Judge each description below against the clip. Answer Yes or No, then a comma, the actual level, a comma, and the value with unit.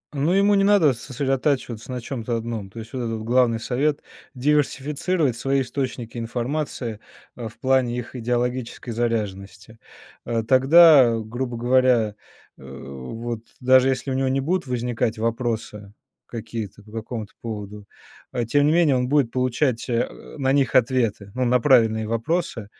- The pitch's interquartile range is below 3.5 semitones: Yes, average, 2.8 semitones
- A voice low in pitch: Yes, low, 120 Hz